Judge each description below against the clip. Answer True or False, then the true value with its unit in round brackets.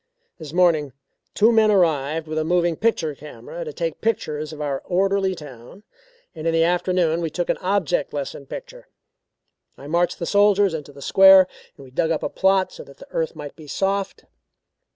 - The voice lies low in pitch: False (170 Hz)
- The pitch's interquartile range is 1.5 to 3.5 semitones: False (4.3 semitones)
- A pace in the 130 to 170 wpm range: False (190 wpm)